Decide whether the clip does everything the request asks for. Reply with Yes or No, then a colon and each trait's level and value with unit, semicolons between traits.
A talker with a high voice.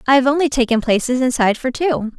Yes: very high, 255 Hz